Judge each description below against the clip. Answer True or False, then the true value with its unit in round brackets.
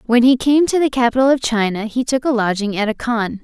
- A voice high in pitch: True (240 Hz)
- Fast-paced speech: True (260 wpm)